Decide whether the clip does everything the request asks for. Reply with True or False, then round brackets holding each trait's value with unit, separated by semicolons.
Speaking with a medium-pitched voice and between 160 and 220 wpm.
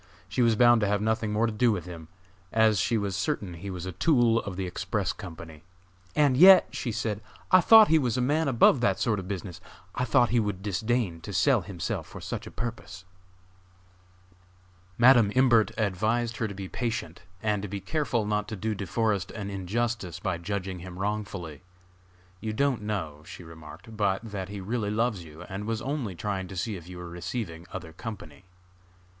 False (105 Hz; 195 wpm)